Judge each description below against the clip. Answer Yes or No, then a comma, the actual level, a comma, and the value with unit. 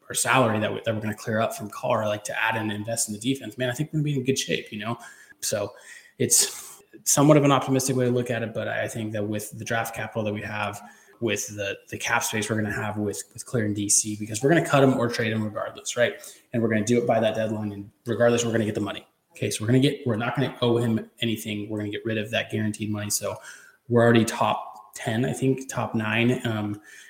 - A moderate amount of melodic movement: Yes, average, 3.1 semitones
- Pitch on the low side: Yes, low, 115 Hz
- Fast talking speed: Yes, fast, 285 wpm